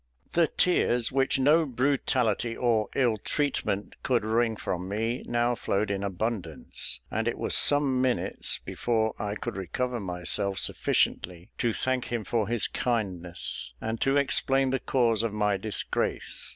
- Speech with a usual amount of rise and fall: Yes, average, 3.9 semitones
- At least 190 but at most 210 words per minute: No, average, 150 wpm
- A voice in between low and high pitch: No, low, 115 Hz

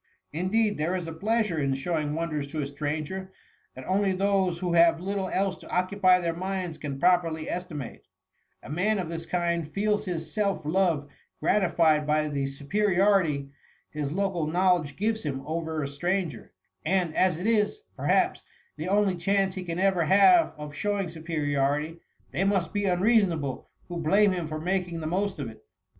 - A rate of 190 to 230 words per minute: No, average, 170 wpm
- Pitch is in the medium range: Yes, medium, 175 Hz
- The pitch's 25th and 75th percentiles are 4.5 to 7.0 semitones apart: No, average, 4.0 semitones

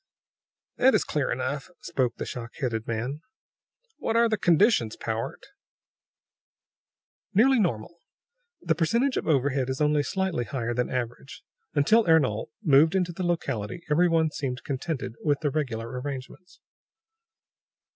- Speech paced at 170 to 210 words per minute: No, slow, 135 wpm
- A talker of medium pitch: Yes, medium, 145 Hz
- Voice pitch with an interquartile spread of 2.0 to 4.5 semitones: No, wide, 5.4 semitones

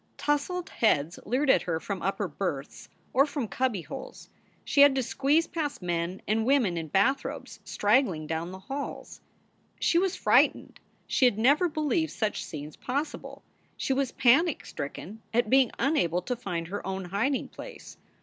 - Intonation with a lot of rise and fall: Yes, wide, 7.7 semitones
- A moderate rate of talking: Yes, average, 160 wpm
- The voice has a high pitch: Yes, high, 235 Hz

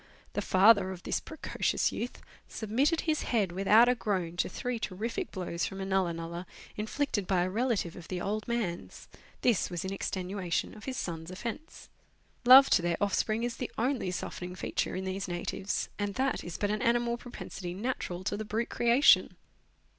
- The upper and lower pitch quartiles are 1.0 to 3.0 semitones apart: No, average, 4.6 semitones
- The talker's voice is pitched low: No, high, 205 Hz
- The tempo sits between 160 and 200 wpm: Yes, average, 185 wpm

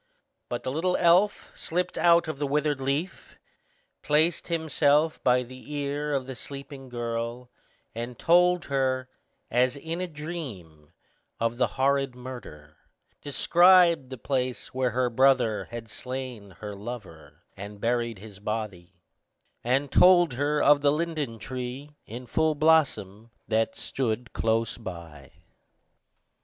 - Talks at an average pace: No, slow, 130 wpm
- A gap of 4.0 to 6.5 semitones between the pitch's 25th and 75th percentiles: Yes, average, 4.6 semitones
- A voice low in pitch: Yes, low, 130 Hz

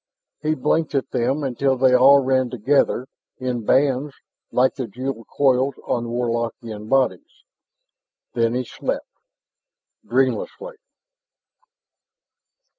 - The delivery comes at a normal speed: No, slow, 105 wpm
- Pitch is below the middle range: Yes, low, 130 Hz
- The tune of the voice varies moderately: No, narrow, 2.2 semitones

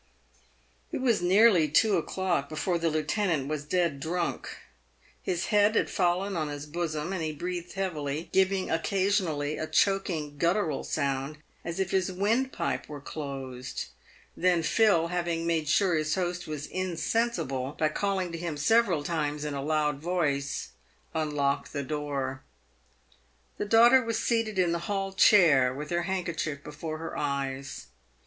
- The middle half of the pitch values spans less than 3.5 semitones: No, average, 4.2 semitones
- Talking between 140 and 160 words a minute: Yes, average, 150 wpm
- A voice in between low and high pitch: Yes, medium, 165 Hz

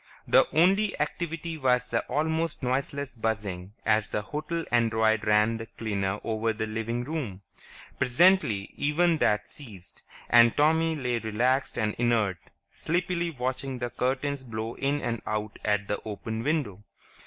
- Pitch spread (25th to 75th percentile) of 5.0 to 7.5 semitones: Yes, wide, 5.4 semitones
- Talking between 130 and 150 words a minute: Yes, average, 145 wpm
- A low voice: Yes, low, 120 Hz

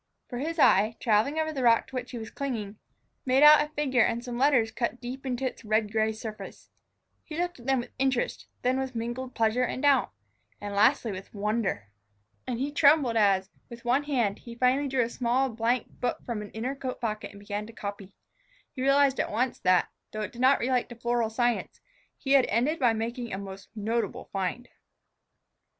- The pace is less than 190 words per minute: No, average, 200 wpm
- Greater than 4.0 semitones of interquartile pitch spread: No, average, 3.2 semitones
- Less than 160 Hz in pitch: No, high, 240 Hz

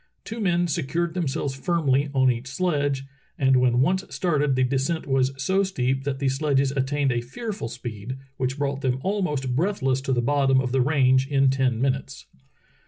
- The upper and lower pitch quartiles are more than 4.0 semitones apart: No, narrow, 2.6 semitones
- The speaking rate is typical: Yes, average, 175 wpm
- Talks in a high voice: No, low, 135 Hz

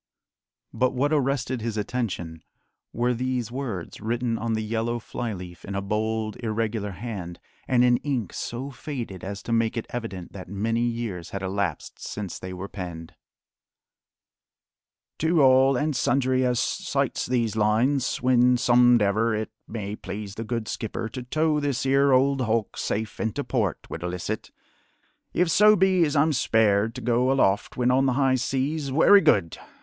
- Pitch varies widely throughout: No, average, 3.7 semitones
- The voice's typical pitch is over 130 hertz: No, low, 115 Hz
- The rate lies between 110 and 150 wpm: No, average, 160 wpm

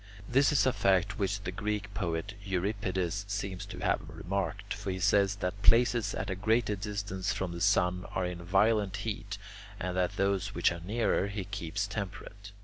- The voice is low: Yes, low, 100 Hz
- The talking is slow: No, average, 185 wpm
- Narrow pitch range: Yes, narrow, 2.0 semitones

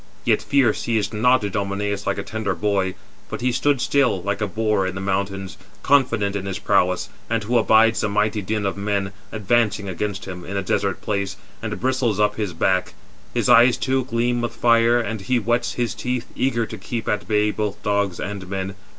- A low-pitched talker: Yes, low, 105 Hz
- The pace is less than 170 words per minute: No, average, 200 wpm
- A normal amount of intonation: Yes, average, 3.0 semitones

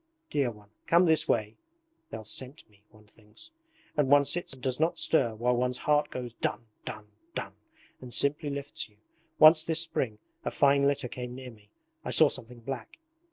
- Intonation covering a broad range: No, average, 4.2 semitones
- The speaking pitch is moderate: No, low, 125 Hz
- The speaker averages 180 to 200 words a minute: Yes, average, 185 wpm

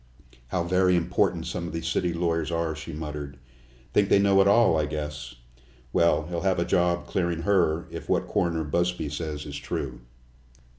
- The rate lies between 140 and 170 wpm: No, average, 180 wpm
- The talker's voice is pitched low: Yes, very low, 85 Hz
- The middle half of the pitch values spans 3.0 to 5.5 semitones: No, narrow, 2.6 semitones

